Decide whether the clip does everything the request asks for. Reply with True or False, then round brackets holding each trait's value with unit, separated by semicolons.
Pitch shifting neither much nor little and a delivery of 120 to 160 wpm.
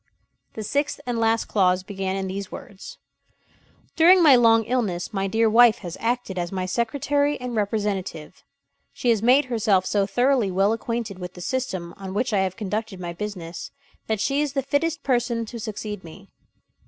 False (4.3 semitones; 180 wpm)